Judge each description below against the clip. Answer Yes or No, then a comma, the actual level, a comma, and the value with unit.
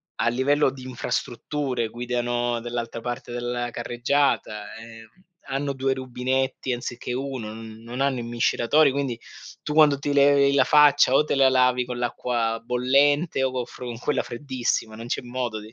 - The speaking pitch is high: No, low, 125 Hz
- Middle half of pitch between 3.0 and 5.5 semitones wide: No, narrow, 2.4 semitones